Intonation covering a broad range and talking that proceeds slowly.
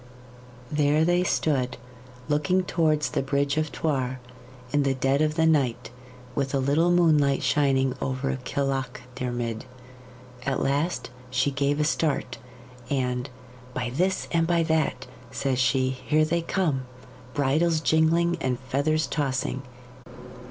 No: average, 3.2 semitones; slow, 130 wpm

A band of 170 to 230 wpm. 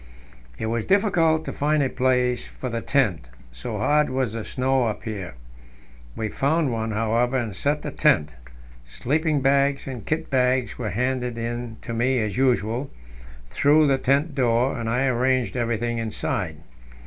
No: average, 160 wpm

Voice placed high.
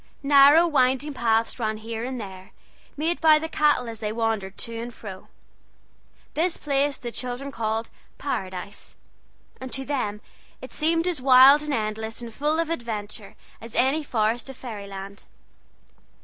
Yes: high, 245 Hz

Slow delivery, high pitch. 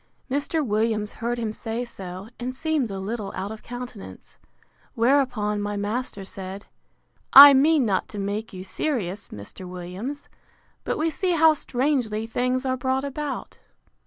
No: average, 150 wpm; high, 230 Hz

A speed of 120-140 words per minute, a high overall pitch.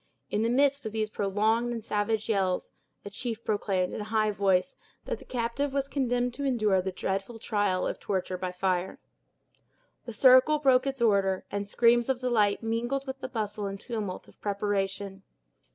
No: average, 180 wpm; high, 215 Hz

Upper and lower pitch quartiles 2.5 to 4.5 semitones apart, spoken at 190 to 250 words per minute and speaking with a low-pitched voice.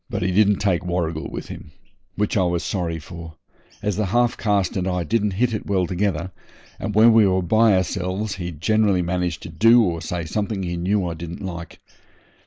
Yes: average, 3.2 semitones; average, 195 wpm; very low, 95 Hz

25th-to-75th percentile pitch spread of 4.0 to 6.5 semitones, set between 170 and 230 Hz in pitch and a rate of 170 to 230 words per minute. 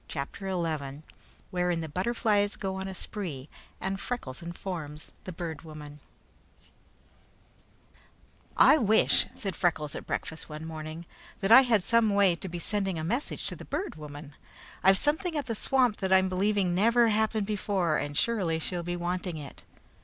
No: average, 4.6 semitones; medium, 185 Hz; average, 160 wpm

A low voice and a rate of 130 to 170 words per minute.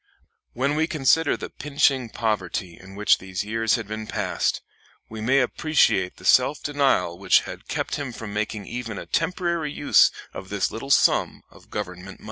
No: low, 115 Hz; average, 180 wpm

